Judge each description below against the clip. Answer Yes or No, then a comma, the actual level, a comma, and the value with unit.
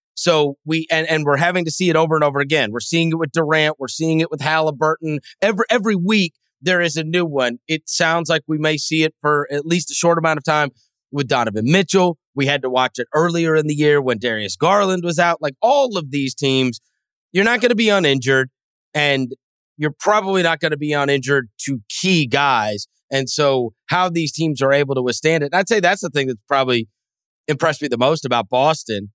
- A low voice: No, medium, 155 Hz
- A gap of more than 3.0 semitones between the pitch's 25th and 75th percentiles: Yes, average, 3.4 semitones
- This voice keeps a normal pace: No, fast, 225 wpm